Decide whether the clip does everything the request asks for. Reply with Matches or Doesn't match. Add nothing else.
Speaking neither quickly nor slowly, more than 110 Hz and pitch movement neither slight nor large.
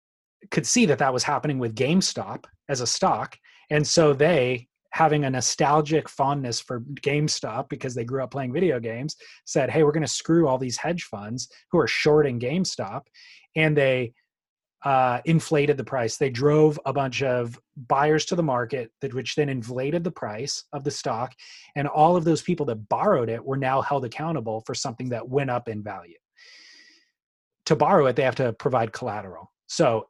Matches